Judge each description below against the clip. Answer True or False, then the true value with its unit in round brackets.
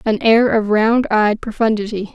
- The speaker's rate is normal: True (170 wpm)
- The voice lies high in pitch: True (220 Hz)